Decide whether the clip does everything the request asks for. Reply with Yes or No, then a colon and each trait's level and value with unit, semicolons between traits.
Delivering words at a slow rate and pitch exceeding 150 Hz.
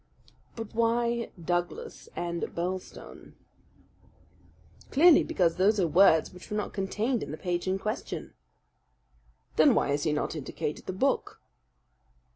Yes: slow, 130 wpm; high, 190 Hz